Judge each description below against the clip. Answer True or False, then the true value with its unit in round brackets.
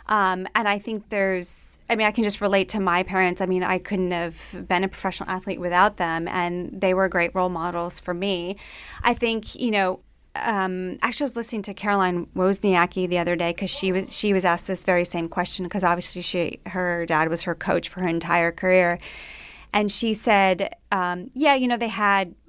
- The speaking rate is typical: False (210 wpm)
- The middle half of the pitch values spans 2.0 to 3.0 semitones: True (2.4 semitones)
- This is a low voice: False (185 Hz)